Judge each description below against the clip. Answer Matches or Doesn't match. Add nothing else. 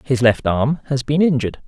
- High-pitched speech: Doesn't match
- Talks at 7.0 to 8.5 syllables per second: Doesn't match